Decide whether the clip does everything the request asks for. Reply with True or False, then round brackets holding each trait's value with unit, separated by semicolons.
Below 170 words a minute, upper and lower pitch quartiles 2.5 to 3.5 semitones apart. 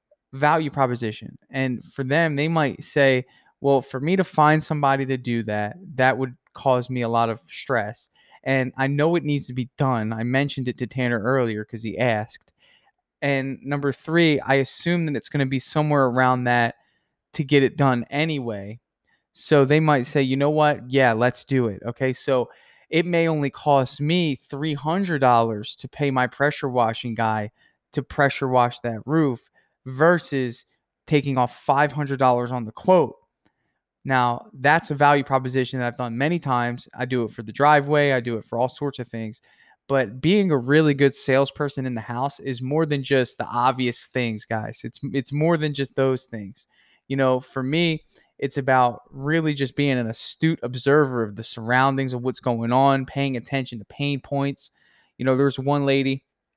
False (185 wpm; 2.8 semitones)